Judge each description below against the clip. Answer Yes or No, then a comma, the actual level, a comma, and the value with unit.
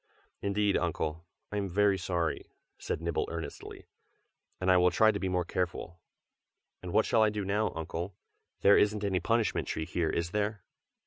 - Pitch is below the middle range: Yes, very low, 95 Hz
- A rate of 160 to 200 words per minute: Yes, average, 180 wpm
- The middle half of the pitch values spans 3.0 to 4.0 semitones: Yes, average, 3.3 semitones